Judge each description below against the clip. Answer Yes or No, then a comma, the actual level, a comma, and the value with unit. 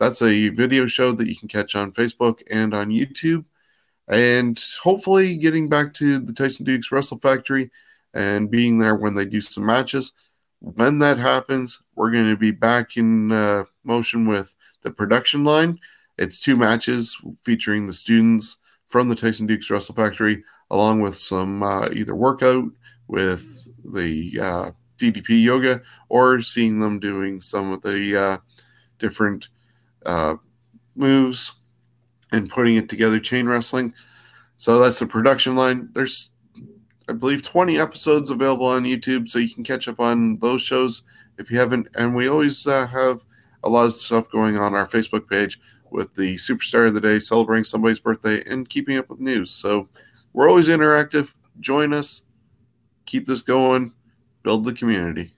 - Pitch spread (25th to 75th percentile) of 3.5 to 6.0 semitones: No, average, 2.9 semitones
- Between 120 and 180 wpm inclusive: Yes, average, 165 wpm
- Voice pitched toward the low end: Yes, low, 120 Hz